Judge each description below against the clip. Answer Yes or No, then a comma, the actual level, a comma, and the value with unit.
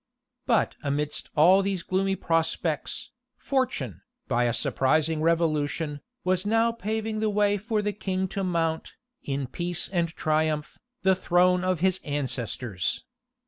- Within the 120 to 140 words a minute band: Yes, slow, 135 wpm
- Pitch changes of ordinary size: Yes, average, 4.5 semitones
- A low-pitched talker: No, medium, 170 Hz